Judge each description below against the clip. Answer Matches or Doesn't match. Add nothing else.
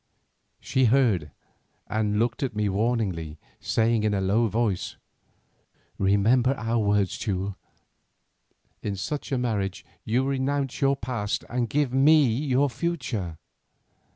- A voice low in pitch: Matches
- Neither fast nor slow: Doesn't match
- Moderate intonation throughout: Matches